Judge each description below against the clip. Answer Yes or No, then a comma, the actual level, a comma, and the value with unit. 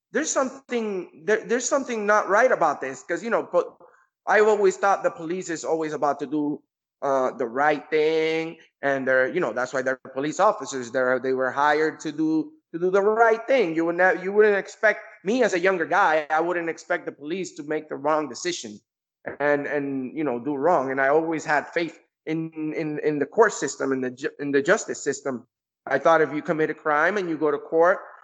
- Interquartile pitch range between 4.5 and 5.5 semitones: Yes, average, 5.1 semitones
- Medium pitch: Yes, medium, 160 Hz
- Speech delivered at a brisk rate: Yes, fast, 220 wpm